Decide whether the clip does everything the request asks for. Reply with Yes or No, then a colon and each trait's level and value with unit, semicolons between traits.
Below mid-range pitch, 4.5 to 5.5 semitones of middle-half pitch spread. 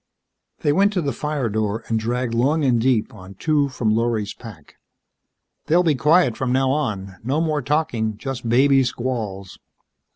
Yes: low, 125 Hz; average, 4.9 semitones